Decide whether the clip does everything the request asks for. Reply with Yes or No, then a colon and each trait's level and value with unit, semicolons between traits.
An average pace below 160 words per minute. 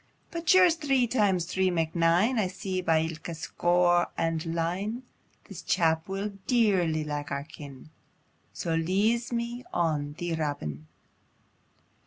Yes: average, 140 wpm